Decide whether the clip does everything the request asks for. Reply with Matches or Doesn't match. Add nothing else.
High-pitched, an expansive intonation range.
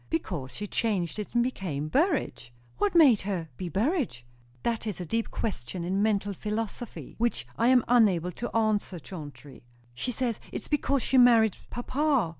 Matches